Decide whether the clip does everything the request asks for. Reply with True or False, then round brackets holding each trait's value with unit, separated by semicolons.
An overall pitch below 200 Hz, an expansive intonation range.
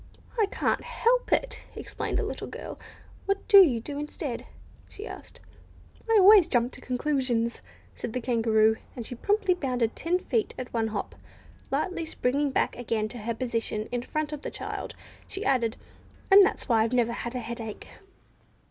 False (250 Hz; 6.7 semitones)